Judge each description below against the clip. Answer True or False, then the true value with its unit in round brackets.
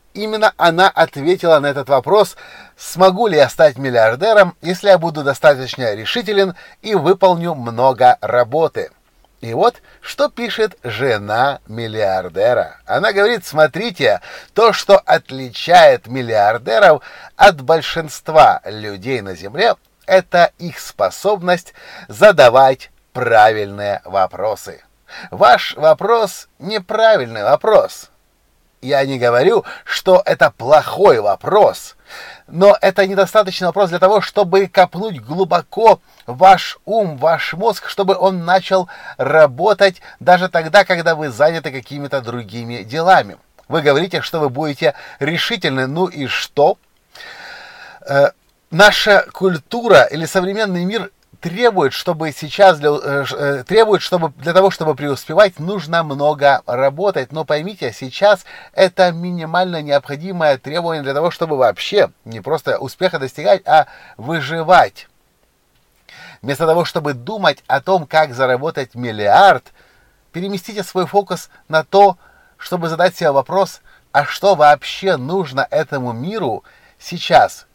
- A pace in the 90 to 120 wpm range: True (115 wpm)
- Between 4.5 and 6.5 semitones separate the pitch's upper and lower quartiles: True (5.3 semitones)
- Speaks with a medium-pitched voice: True (170 Hz)